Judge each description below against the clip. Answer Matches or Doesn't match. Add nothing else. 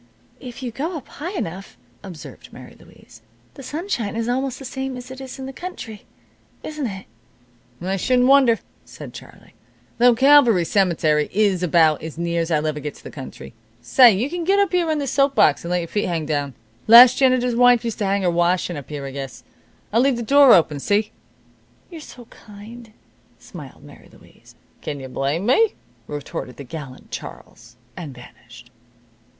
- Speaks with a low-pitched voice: Doesn't match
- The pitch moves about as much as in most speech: Doesn't match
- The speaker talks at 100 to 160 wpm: Doesn't match